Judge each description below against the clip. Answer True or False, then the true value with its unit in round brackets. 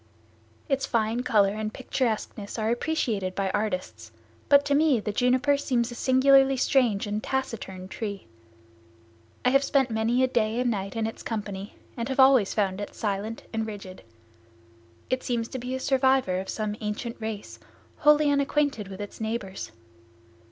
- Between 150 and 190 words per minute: True (160 wpm)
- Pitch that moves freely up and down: False (4.2 semitones)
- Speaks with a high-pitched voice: True (225 Hz)